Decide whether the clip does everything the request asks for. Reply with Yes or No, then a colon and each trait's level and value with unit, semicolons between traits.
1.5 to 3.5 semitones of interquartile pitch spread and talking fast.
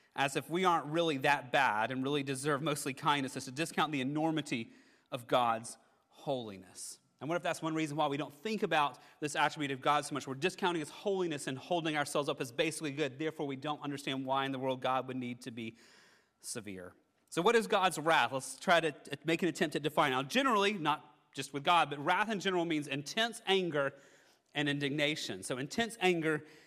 Yes: average, 3.2 semitones; fast, 210 wpm